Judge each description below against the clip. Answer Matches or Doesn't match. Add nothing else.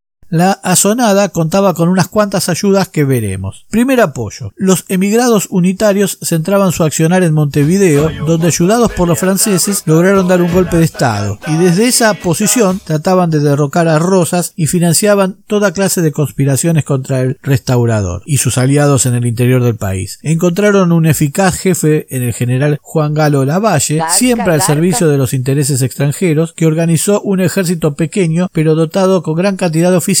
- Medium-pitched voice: Matches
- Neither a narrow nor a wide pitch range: Matches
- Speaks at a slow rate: Doesn't match